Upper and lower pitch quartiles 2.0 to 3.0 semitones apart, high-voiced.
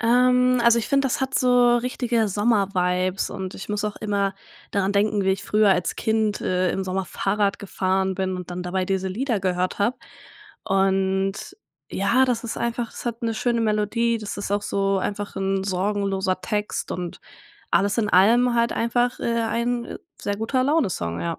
No: average, 3.5 semitones; high, 205 Hz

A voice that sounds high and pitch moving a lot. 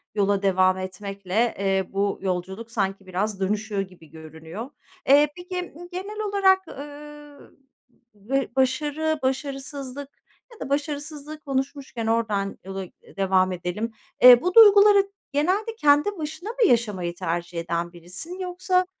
Yes: high, 245 Hz; wide, 7.9 semitones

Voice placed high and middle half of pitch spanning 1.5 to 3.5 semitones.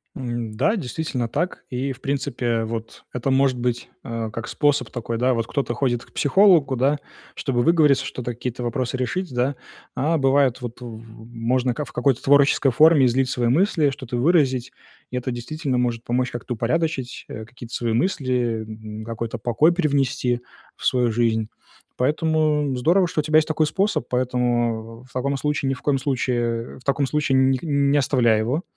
No: low, 130 Hz; average, 3.1 semitones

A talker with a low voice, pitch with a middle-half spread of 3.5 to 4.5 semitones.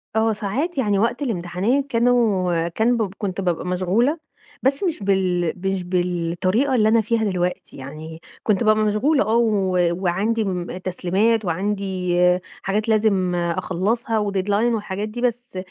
No: high, 205 Hz; average, 4.0 semitones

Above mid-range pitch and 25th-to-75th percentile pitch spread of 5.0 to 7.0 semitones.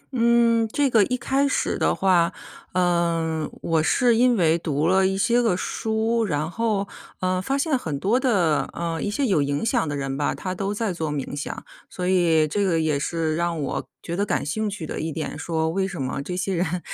No: medium, 180 Hz; wide, 5.5 semitones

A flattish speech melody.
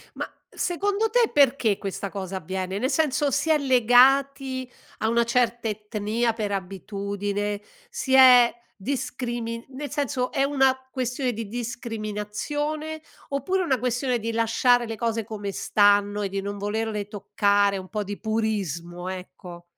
No: average, 4.4 semitones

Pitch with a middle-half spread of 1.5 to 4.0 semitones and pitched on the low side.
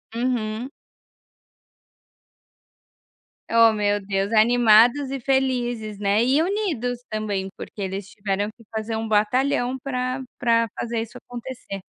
No: average, 3.0 semitones; high, 230 Hz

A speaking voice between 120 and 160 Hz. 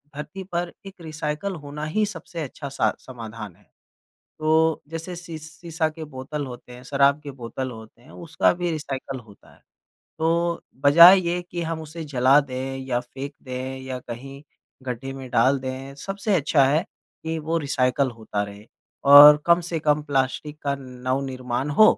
Yes: medium, 140 Hz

